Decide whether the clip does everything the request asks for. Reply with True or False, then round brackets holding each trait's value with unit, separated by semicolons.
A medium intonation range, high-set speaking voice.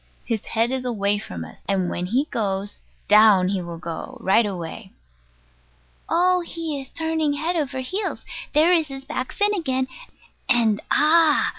False (7.8 semitones; 255 Hz)